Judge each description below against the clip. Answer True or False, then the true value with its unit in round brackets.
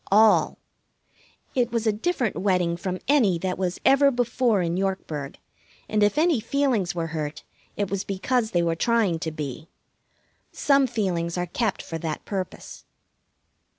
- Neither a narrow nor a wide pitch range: False (5.7 semitones)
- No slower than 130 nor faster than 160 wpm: True (150 wpm)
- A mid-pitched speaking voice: False (195 Hz)